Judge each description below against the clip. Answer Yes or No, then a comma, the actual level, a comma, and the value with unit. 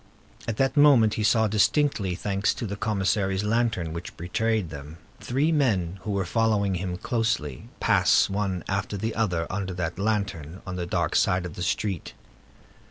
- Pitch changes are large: No, average, 3.8 semitones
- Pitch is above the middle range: No, low, 100 Hz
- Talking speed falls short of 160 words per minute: No, average, 165 wpm